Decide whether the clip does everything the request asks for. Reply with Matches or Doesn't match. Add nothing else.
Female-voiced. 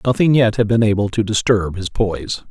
Doesn't match